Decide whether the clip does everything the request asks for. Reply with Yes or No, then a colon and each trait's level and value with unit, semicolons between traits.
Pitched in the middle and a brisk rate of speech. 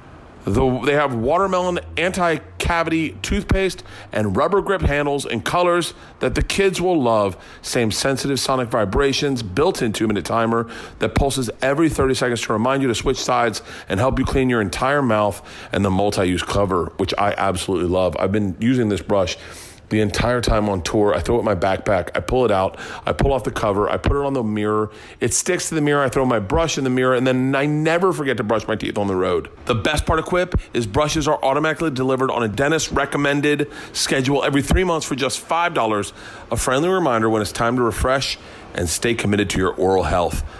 No: low, 130 Hz; fast, 215 wpm